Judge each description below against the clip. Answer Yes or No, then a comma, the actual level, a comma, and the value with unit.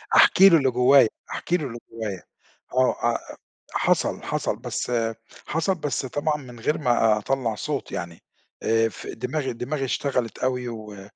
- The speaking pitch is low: Yes, low, 125 Hz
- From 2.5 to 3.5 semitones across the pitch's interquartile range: No, average, 4.0 semitones